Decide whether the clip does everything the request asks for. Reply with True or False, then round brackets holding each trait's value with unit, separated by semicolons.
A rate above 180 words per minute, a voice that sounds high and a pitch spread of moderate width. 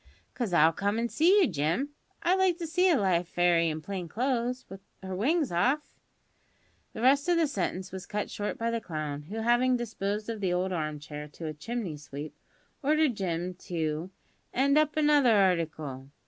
False (190 wpm; 200 Hz; 7.5 semitones)